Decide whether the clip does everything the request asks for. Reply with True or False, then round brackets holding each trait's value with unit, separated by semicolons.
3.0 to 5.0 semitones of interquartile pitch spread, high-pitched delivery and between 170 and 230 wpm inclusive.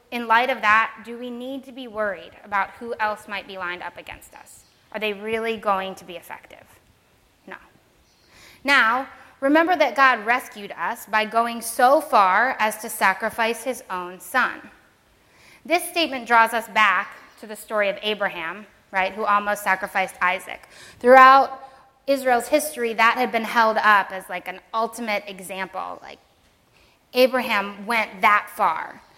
False (3.8 semitones; 225 Hz; 155 wpm)